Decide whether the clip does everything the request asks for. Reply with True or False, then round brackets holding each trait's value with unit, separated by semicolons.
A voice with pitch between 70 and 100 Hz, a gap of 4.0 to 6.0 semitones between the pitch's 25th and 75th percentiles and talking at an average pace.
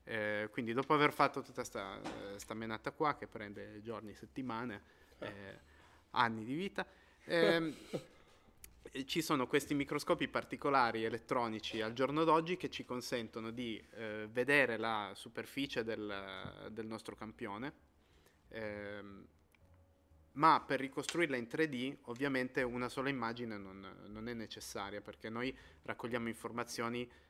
False (115 Hz; 4.3 semitones; 130 wpm)